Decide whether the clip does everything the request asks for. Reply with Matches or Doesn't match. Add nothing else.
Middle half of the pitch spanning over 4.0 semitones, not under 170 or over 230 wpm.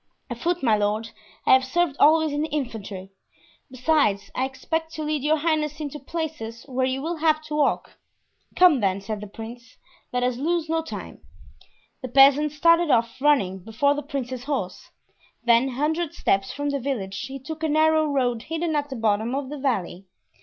Matches